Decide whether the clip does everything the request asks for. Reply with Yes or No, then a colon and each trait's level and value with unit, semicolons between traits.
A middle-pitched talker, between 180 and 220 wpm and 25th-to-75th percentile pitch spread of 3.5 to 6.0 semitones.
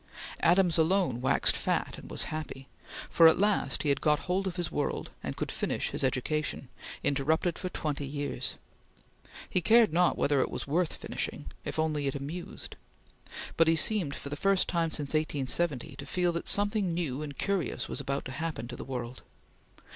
Yes: medium, 155 Hz; average, 185 wpm; average, 4.0 semitones